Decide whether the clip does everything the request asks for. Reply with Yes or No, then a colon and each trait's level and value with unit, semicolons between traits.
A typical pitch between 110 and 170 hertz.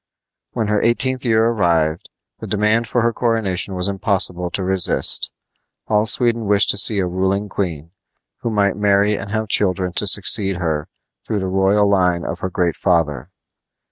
No: low, 100 Hz